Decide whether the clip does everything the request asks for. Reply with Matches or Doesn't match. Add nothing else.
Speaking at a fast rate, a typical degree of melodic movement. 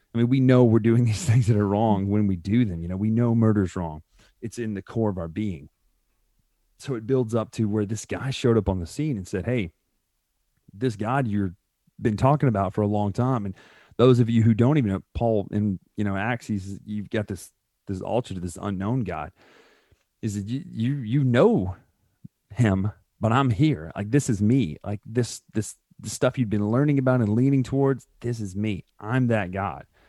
Matches